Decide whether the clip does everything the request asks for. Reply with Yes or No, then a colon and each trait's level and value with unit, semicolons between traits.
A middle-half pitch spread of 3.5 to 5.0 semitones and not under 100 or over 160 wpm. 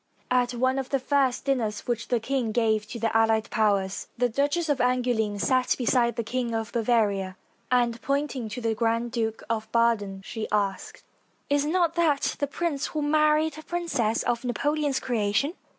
No: average, 3.9 semitones; average, 175 wpm